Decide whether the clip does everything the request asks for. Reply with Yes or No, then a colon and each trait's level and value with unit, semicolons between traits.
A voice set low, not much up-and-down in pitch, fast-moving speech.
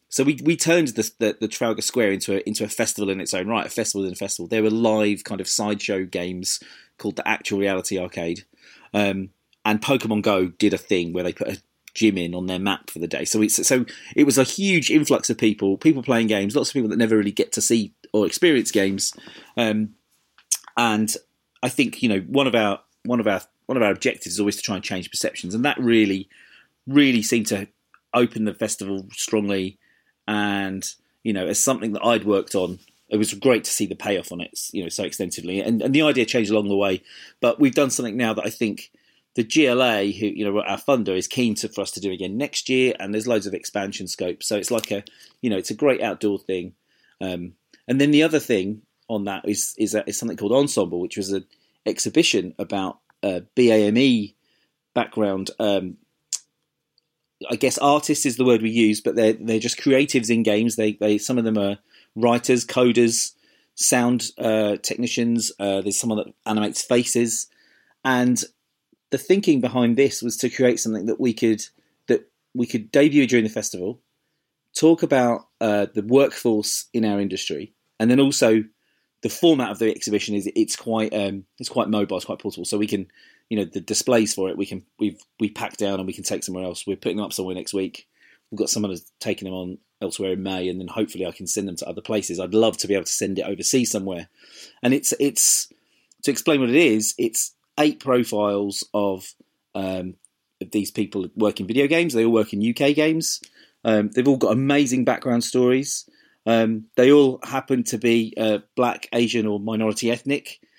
No: low, 110 Hz; average, 3.5 semitones; fast, 210 wpm